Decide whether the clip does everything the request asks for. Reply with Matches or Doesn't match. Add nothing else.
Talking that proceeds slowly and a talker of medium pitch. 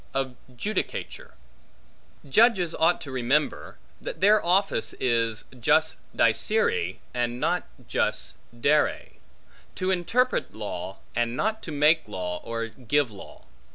Matches